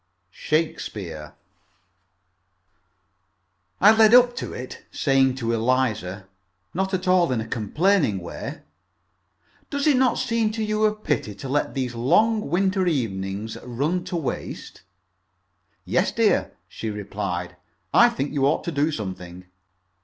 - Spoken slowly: Yes, slow, 130 wpm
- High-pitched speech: No, low, 135 Hz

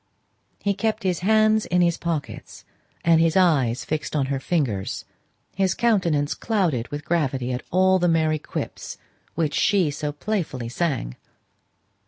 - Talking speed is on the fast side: No, average, 145 wpm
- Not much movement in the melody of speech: No, average, 4.6 semitones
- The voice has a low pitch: No, medium, 165 Hz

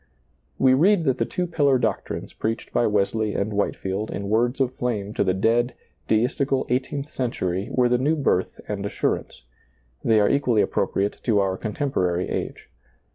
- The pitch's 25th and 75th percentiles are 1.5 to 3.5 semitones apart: No, average, 4.5 semitones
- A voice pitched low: Yes, low, 115 Hz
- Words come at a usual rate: Yes, average, 165 wpm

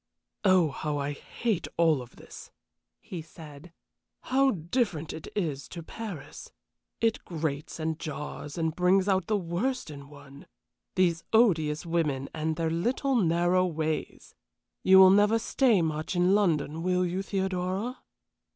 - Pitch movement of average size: Yes, average, 3.8 semitones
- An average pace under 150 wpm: Yes, average, 140 wpm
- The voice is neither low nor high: Yes, medium, 170 Hz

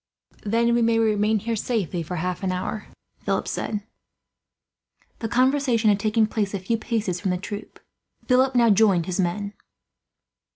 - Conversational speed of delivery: Yes, average, 160 wpm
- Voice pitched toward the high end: Yes, high, 215 Hz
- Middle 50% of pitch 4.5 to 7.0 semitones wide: No, average, 3.2 semitones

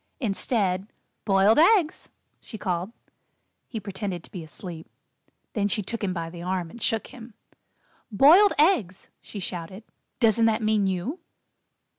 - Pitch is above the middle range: Yes, high, 205 Hz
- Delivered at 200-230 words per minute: No, average, 140 wpm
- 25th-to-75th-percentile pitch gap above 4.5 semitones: No, average, 3.9 semitones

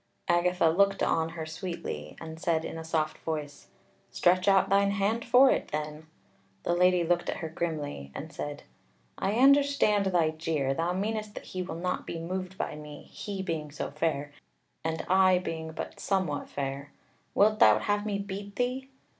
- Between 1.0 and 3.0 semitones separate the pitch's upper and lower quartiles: No, average, 4.0 semitones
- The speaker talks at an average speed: Yes, average, 175 wpm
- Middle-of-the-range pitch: Yes, medium, 175 Hz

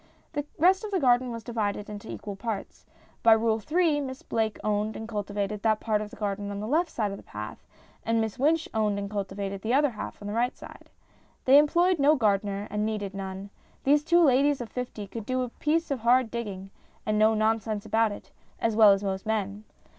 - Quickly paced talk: Yes, fast, 215 wpm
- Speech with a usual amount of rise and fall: Yes, average, 4.0 semitones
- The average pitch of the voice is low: No, high, 220 Hz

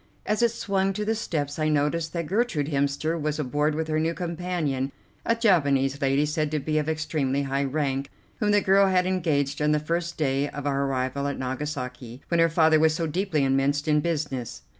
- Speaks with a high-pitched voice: No, medium, 150 Hz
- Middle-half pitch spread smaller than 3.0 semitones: No, average, 3.3 semitones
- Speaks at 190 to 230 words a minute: Yes, fast, 205 wpm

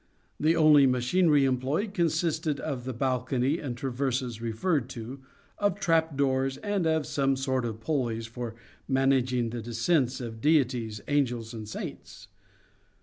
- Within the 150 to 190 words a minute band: No, average, 140 wpm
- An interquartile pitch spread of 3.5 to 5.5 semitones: Yes, average, 4.2 semitones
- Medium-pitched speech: No, low, 130 Hz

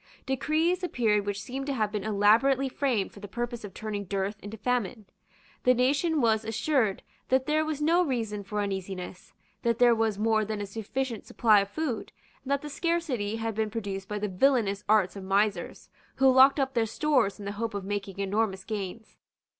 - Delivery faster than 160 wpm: Yes, average, 195 wpm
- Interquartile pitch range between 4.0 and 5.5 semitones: Yes, average, 4.5 semitones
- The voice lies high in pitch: Yes, high, 220 Hz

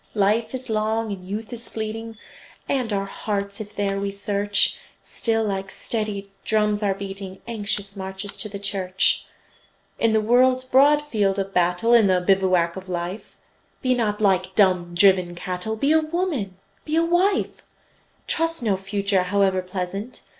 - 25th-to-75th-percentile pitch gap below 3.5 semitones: Yes, average, 2.8 semitones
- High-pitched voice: Yes, high, 205 Hz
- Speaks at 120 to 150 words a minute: No, average, 160 wpm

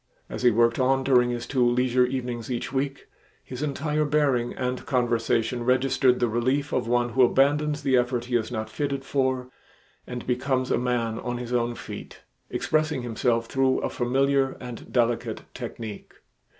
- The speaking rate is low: No, average, 165 wpm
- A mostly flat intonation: Yes, narrow, 1.8 semitones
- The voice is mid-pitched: No, low, 125 Hz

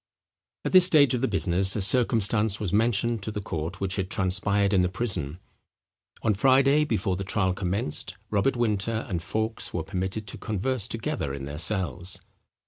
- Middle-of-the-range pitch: No, low, 100 Hz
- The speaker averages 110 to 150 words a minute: No, average, 175 wpm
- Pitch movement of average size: Yes, average, 3.6 semitones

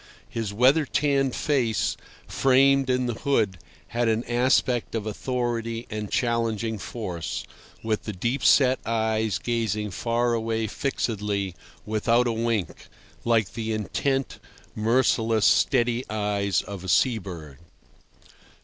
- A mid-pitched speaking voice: No, low, 115 Hz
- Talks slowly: Yes, slow, 120 wpm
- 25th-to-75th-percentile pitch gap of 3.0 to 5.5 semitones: No, narrow, 2.4 semitones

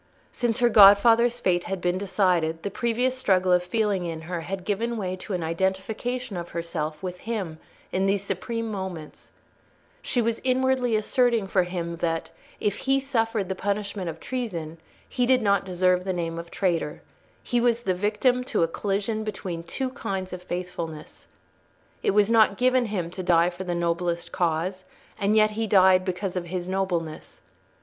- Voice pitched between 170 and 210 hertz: Yes, high, 190 Hz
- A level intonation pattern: No, average, 4.1 semitones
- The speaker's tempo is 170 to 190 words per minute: Yes, average, 175 wpm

